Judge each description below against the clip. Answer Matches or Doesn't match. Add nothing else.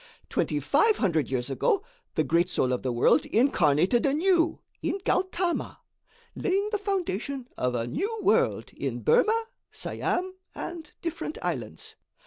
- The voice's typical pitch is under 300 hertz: Doesn't match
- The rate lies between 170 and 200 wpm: Doesn't match